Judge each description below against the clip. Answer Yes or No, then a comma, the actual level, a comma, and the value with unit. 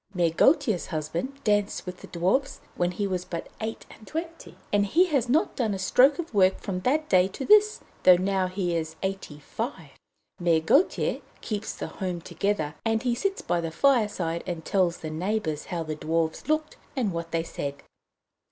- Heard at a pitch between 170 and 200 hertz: Yes, high, 190 Hz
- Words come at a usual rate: Yes, average, 190 wpm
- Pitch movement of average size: No, wide, 6.3 semitones